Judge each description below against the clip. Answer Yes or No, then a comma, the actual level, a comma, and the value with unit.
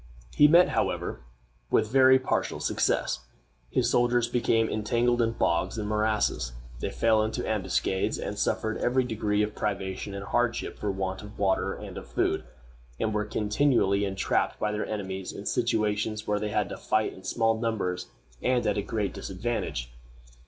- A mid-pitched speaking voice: No, low, 105 Hz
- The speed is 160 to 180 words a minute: Yes, average, 165 wpm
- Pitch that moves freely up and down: No, narrow, 2.6 semitones